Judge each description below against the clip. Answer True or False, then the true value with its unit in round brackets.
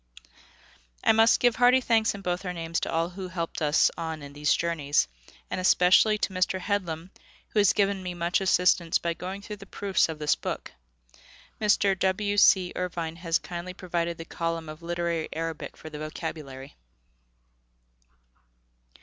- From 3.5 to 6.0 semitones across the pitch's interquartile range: False (2.8 semitones)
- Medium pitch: True (175 Hz)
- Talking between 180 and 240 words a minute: False (165 wpm)